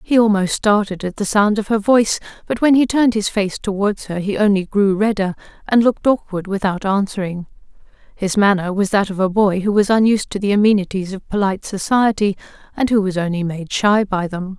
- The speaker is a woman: Yes, female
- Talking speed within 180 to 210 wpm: Yes, fast, 205 wpm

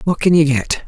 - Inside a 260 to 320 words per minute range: Yes, fast, 275 wpm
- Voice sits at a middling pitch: Yes, medium, 155 Hz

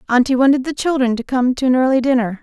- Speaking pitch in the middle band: No, very high, 255 Hz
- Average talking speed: No, fast, 245 wpm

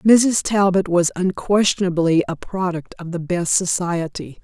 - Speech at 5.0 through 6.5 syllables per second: No, 4.2 syllables/s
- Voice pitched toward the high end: No, medium, 180 Hz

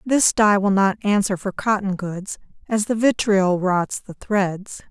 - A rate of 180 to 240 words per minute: No, average, 170 wpm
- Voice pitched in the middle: No, high, 200 Hz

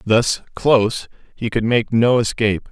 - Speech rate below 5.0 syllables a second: Yes, 4.5 syllables/s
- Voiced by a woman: No, male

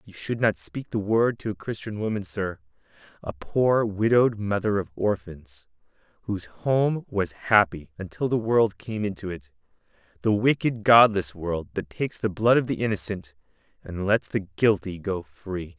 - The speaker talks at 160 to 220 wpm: Yes, average, 165 wpm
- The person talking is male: Yes, male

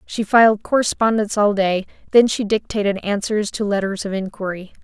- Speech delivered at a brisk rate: No, average, 160 wpm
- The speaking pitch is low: No, high, 205 Hz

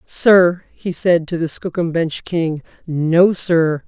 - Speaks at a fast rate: No, average, 155 wpm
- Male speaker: No, female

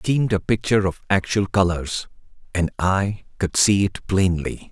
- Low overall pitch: Yes, very low, 95 Hz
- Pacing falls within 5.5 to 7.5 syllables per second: No, 4.8 syllables/s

